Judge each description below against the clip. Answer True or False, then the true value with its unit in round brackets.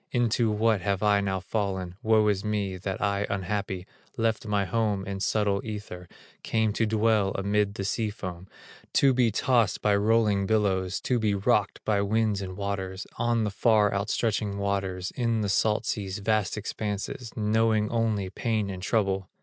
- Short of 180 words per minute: True (165 wpm)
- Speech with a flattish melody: True (2.0 semitones)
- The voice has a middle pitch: False (105 Hz)